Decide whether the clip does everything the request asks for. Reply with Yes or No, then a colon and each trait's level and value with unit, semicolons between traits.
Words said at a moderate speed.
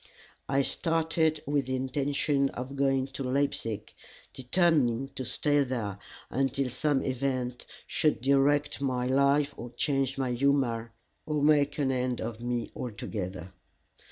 No: slow, 130 wpm